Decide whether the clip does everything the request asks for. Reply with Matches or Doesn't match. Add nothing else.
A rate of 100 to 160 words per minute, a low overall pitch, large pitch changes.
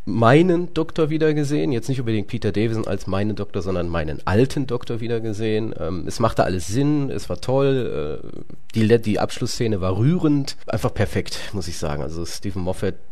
Doesn't match